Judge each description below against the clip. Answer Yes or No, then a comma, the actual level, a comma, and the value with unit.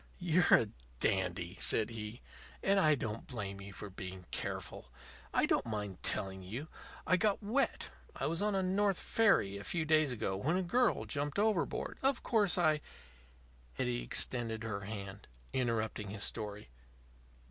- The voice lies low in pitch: Yes, low, 115 Hz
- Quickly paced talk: No, average, 165 wpm